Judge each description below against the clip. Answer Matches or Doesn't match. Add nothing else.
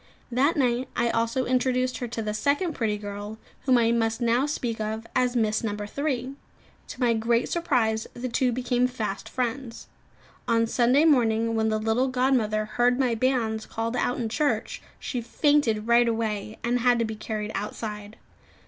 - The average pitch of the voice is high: Matches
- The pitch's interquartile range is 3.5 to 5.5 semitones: Doesn't match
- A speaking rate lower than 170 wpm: Doesn't match